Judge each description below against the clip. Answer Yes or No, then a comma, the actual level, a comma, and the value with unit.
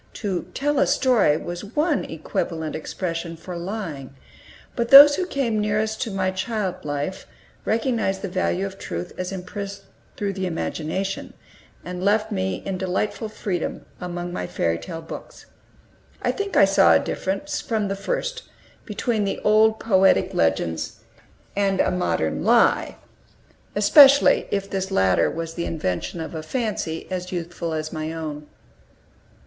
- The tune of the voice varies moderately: Yes, average, 4.5 semitones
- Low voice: No, high, 190 Hz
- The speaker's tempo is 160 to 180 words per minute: No, average, 150 wpm